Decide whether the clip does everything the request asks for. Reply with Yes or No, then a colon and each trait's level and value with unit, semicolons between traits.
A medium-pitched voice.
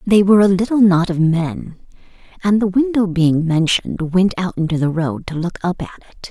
Yes: medium, 180 Hz